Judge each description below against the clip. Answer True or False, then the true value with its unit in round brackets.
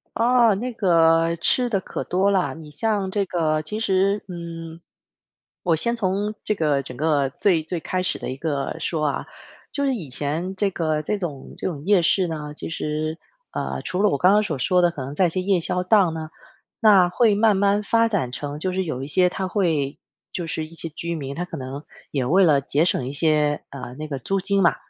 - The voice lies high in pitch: False (170 Hz)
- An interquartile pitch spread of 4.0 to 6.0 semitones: True (4.4 semitones)